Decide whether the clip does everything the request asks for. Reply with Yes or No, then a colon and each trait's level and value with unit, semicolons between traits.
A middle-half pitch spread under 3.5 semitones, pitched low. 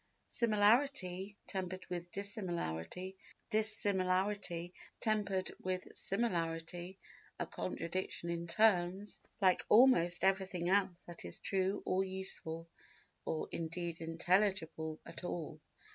No: average, 2.7 semitones; medium, 185 Hz